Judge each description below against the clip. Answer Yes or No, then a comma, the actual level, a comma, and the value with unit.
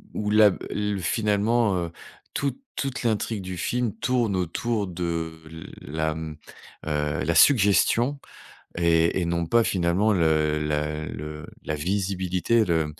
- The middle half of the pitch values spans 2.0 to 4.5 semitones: No, average, 5.0 semitones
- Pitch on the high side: No, very low, 90 Hz